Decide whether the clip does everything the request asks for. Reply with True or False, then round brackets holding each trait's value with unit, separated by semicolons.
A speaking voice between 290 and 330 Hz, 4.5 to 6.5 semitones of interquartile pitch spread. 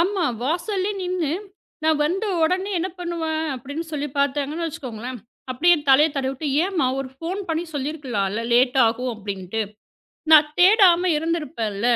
True (300 Hz; 5.2 semitones)